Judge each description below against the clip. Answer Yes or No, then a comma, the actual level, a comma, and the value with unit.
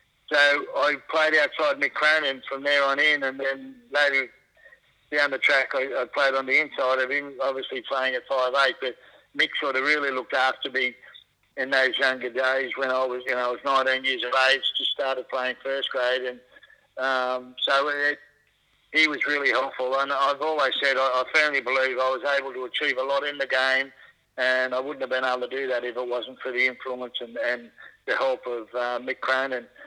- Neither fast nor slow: No, fast, 215 wpm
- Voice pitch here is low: Yes, low, 130 Hz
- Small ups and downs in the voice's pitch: Yes, narrow, 1.3 semitones